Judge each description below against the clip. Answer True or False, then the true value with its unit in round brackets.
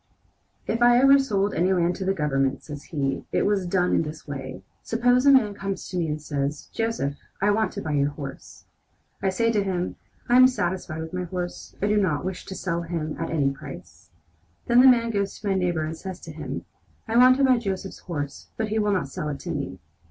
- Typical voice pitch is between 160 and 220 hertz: True (185 Hz)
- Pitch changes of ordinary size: False (5.8 semitones)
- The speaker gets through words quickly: True (230 wpm)